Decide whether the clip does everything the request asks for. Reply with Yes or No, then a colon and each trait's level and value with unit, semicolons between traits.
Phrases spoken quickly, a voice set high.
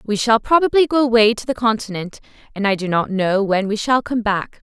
Yes: fast, 230 wpm; high, 220 Hz